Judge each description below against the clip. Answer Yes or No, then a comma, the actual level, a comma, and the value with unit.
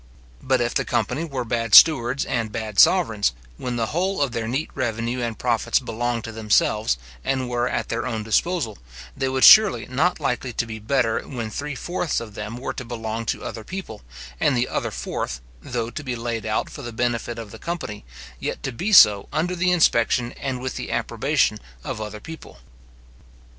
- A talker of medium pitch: No, low, 120 Hz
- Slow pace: No, average, 195 wpm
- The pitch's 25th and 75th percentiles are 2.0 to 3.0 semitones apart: No, average, 3.5 semitones